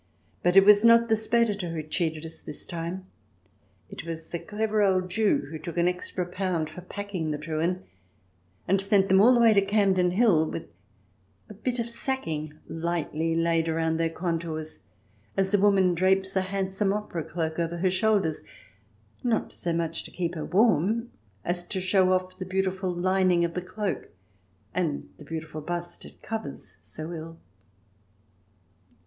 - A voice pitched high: No, medium, 180 Hz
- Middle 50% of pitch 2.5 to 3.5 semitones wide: Yes, average, 3.2 semitones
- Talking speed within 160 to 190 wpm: Yes, average, 170 wpm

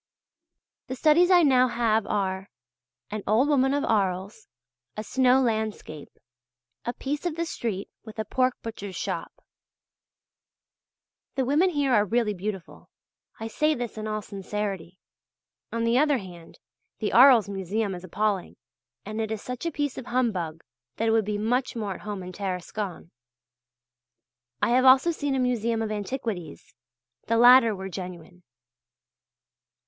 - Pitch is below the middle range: No, high, 220 Hz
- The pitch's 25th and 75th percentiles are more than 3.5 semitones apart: Yes, average, 4.5 semitones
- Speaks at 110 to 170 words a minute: Yes, average, 150 wpm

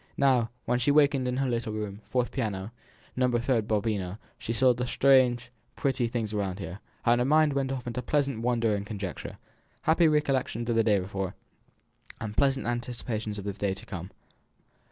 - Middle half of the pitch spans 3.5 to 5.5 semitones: Yes, average, 3.8 semitones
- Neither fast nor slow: Yes, average, 180 wpm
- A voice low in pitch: Yes, low, 120 Hz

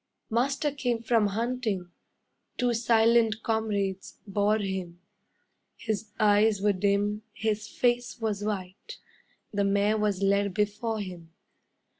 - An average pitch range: No, narrow, 2.2 semitones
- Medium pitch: No, high, 210 Hz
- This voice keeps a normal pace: No, slow, 115 wpm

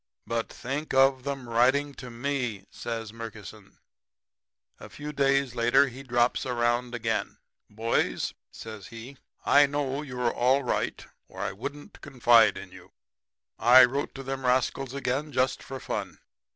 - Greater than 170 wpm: No, average, 150 wpm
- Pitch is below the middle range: Yes, low, 125 Hz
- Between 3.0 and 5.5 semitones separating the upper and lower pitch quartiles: No, narrow, 2.6 semitones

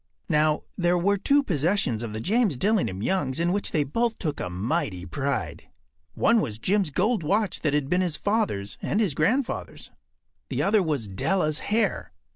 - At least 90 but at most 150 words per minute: No, average, 175 wpm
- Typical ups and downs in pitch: No, wide, 6.9 semitones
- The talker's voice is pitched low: No, medium, 170 Hz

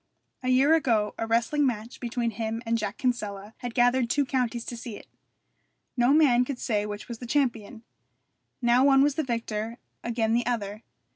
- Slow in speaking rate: No, average, 185 wpm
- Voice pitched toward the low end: No, high, 235 Hz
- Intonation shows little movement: Yes, narrow, 2.3 semitones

